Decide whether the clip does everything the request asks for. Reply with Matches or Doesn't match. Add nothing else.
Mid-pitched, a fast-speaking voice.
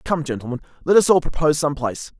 Matches